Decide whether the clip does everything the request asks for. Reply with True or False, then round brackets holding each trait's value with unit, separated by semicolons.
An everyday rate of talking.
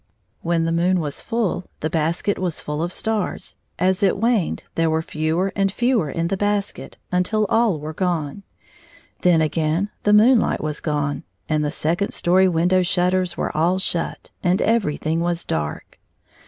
True (170 wpm)